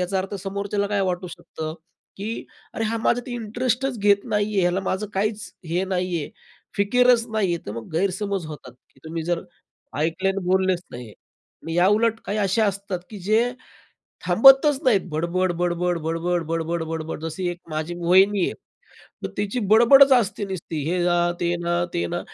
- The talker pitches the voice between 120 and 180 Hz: No, high, 190 Hz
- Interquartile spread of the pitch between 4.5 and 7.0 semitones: No, average, 3.5 semitones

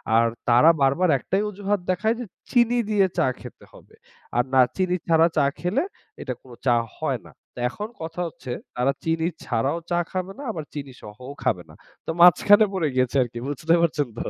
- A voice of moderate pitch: Yes, medium, 165 Hz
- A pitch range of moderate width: No, wide, 6.7 semitones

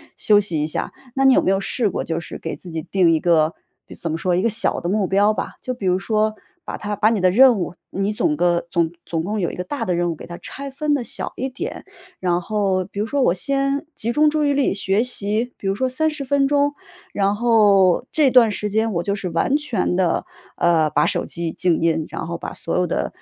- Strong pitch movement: Yes, wide, 6.4 semitones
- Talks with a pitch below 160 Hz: No, high, 205 Hz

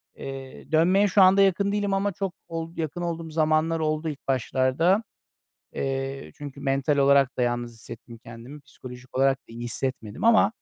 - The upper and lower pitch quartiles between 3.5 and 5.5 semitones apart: Yes, average, 4.7 semitones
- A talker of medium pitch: Yes, medium, 145 Hz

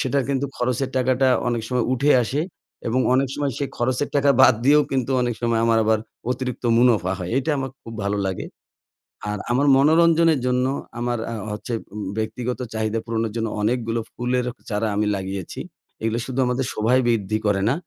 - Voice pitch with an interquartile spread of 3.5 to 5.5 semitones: No, average, 3.0 semitones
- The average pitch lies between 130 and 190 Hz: No, low, 120 Hz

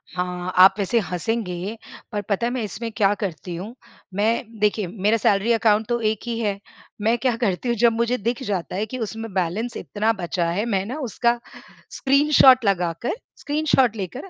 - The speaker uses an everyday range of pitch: Yes, average, 3.5 semitones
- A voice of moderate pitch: No, high, 215 Hz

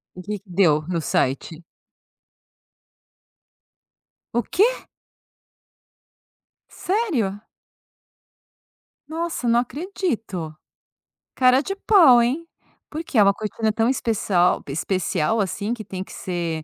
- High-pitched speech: Yes, high, 220 Hz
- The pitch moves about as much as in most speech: No, wide, 7.2 semitones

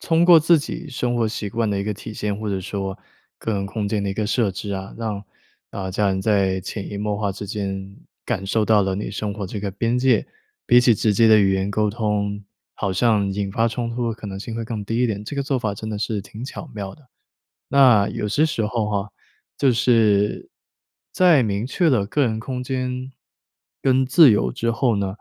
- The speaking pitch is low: Yes, low, 105 Hz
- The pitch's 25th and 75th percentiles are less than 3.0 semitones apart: No, average, 3.3 semitones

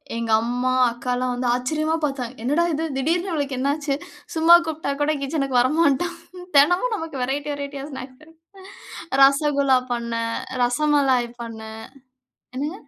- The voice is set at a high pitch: Yes, very high, 275 Hz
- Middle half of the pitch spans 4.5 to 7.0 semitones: No, average, 3.7 semitones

